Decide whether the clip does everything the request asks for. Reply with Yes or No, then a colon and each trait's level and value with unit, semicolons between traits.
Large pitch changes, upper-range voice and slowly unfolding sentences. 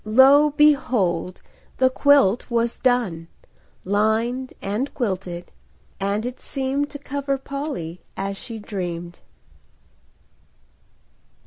Yes: wide, 6.2 semitones; high, 230 Hz; slow, 90 wpm